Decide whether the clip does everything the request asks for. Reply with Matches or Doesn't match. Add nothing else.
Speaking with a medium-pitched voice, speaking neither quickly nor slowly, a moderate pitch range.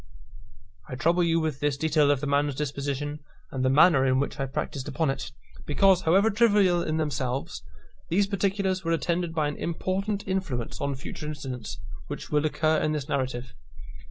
Matches